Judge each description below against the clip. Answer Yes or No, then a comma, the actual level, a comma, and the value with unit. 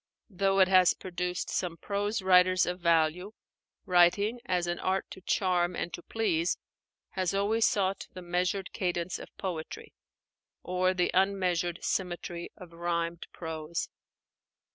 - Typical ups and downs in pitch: No, narrow, 1.6 semitones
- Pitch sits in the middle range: Yes, medium, 180 Hz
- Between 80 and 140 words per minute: Yes, slow, 135 wpm